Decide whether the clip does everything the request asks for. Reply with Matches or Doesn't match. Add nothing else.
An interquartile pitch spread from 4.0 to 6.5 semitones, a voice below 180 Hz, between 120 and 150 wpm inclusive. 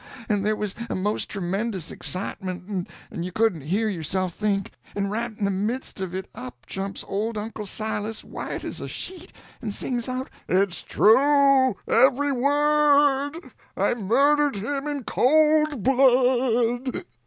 Doesn't match